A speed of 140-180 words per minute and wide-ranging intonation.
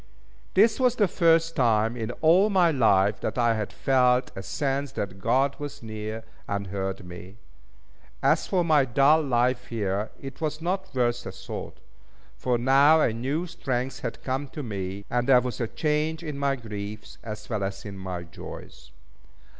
Yes: average, 175 wpm; wide, 5.8 semitones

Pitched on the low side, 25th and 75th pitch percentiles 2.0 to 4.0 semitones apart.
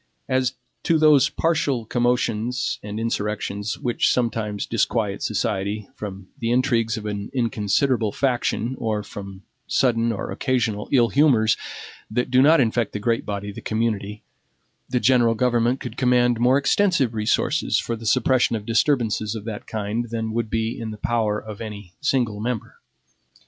Yes: low, 115 Hz; average, 2.8 semitones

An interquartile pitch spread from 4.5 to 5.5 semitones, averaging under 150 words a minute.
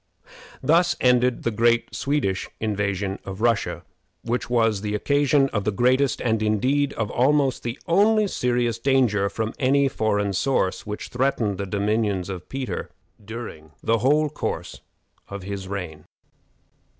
Yes: average, 4.8 semitones; average, 140 wpm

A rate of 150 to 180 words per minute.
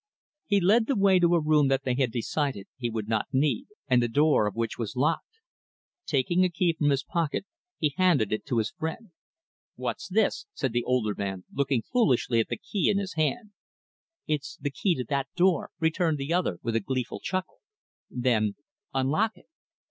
No: average, 195 wpm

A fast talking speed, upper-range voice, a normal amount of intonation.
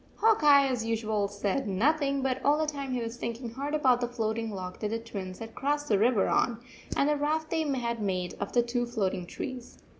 Yes: fast, 220 wpm; high, 240 Hz; average, 4.3 semitones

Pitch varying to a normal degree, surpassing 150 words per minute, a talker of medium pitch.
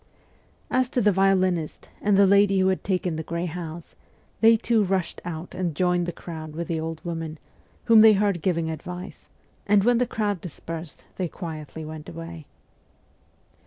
Yes: average, 3.4 semitones; average, 170 wpm; medium, 180 Hz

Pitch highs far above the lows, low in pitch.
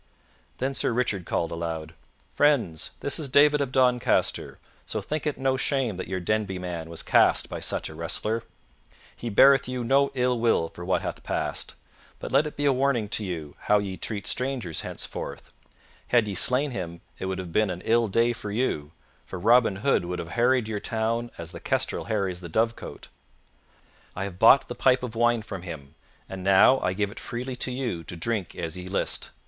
Yes: wide, 5.8 semitones; low, 110 Hz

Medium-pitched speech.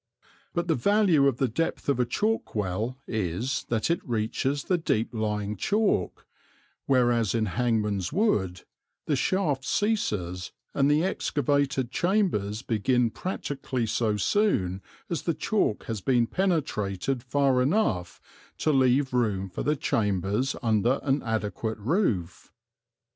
No: low, 125 Hz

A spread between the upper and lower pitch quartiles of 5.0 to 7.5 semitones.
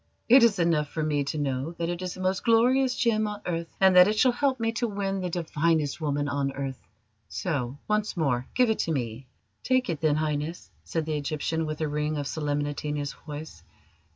Yes: wide, 5.5 semitones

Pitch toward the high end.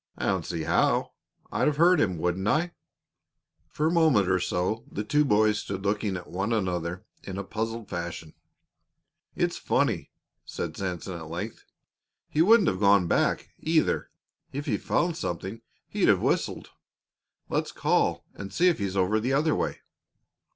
No: low, 105 Hz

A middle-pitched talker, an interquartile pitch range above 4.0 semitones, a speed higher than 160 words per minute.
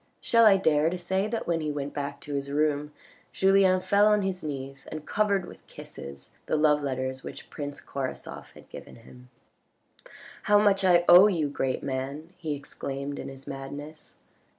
Yes: medium, 150 Hz; average, 5.1 semitones; average, 180 wpm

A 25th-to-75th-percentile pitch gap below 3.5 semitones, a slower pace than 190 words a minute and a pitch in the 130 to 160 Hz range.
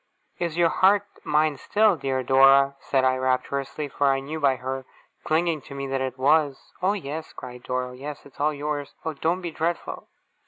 No: average, 3.1 semitones; average, 195 wpm; medium, 140 Hz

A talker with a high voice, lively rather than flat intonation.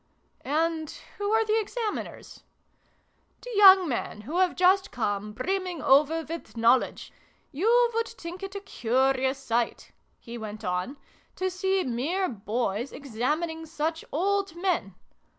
Yes: very high, 320 Hz; wide, 7.5 semitones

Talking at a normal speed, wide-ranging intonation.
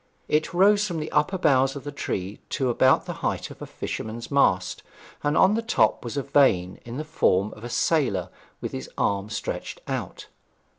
Yes: average, 195 wpm; wide, 6.3 semitones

